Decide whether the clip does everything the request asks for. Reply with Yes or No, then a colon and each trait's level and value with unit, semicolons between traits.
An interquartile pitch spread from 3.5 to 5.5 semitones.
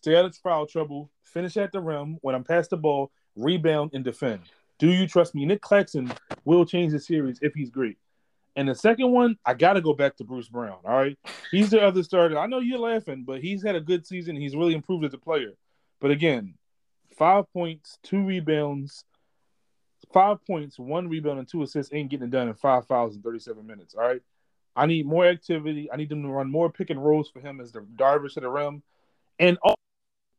Yes: average, 4.3 semitones